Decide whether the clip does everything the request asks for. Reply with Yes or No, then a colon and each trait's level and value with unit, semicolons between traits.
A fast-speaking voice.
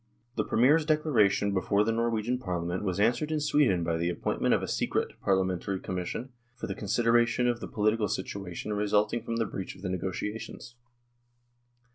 No: average, 170 wpm